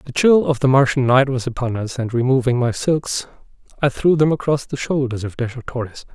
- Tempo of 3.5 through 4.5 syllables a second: No, 5.4 syllables/s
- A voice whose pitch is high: No, low, 130 Hz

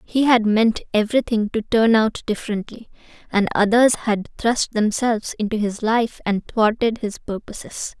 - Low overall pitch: No, high, 220 Hz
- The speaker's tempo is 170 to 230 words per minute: No, average, 150 wpm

